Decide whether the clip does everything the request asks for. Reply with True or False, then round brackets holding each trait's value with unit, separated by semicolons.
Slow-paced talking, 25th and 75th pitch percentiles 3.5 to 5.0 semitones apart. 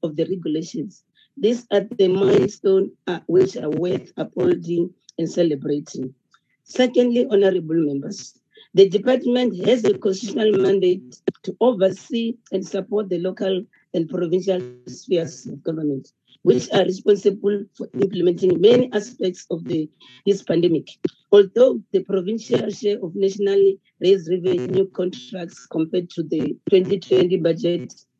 False (125 wpm; 3.0 semitones)